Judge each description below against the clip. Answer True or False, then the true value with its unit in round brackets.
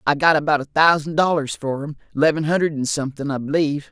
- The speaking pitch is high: False (145 Hz)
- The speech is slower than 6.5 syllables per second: False (6.6 syllables/s)